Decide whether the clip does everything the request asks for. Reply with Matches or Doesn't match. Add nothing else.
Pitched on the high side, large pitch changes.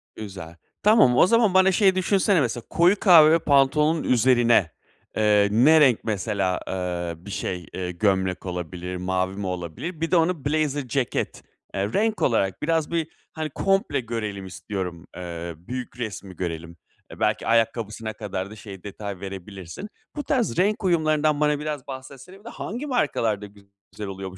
Doesn't match